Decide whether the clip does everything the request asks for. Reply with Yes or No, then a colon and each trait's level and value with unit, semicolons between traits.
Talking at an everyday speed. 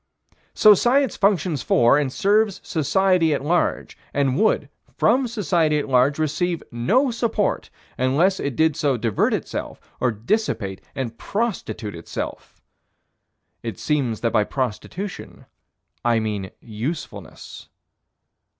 No: slow, 120 wpm